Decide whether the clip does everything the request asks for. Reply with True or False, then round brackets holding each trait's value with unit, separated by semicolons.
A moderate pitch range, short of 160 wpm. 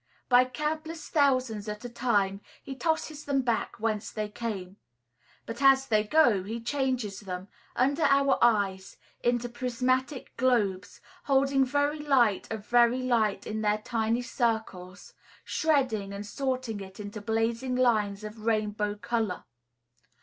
True (3.8 semitones; 135 wpm)